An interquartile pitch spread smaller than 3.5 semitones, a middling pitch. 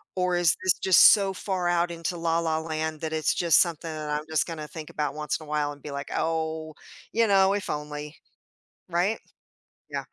Yes: narrow, 2.5 semitones; medium, 160 Hz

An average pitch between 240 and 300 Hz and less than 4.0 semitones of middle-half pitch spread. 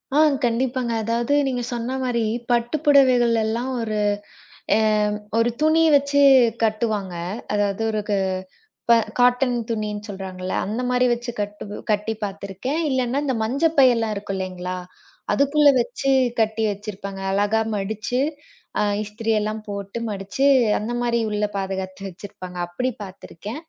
No: high, 225 Hz; average, 3.6 semitones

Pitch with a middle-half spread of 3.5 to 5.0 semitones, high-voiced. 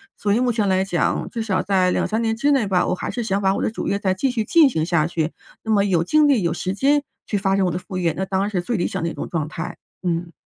Yes: average, 3.9 semitones; high, 195 Hz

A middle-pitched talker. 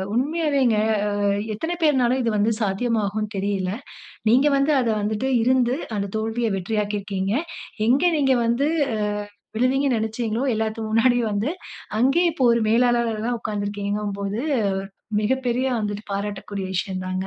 No: high, 225 Hz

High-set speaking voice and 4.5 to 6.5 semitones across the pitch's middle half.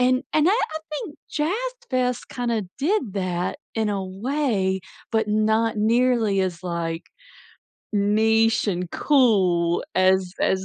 Yes: high, 215 Hz; average, 5.0 semitones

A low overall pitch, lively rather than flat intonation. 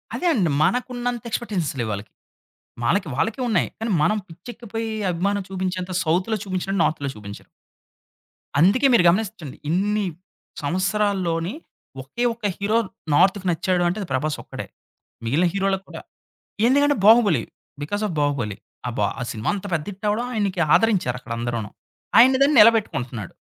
No: high, 190 Hz; wide, 5.7 semitones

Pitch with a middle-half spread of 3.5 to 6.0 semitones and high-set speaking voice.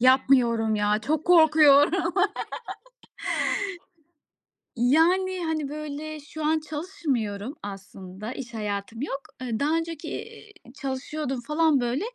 Yes: average, 5.1 semitones; very high, 280 Hz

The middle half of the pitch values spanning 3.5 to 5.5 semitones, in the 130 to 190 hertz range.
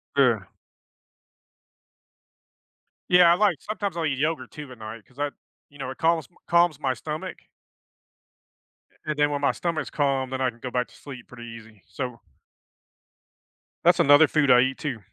Yes: average, 3.8 semitones; medium, 140 Hz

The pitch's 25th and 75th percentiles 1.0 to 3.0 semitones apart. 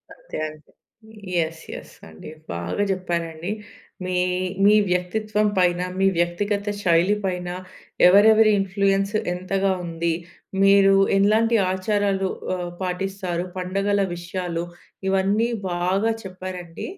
Yes: narrow, 2.5 semitones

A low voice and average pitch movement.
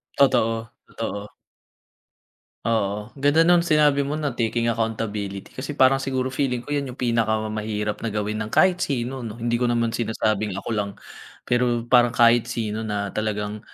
Yes: low, 115 Hz; average, 3.3 semitones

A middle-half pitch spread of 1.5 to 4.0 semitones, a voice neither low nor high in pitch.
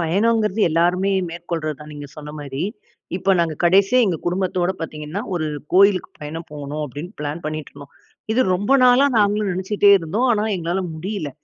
No: average, 4.4 semitones; medium, 175 Hz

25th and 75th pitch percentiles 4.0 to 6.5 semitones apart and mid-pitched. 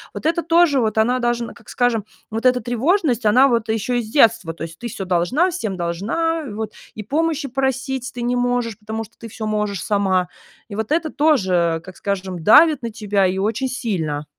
No: average, 4.7 semitones; high, 230 Hz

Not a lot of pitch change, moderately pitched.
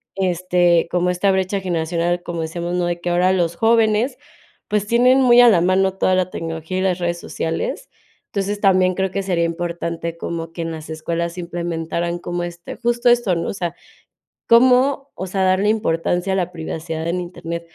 Yes: narrow, 2.3 semitones; medium, 175 Hz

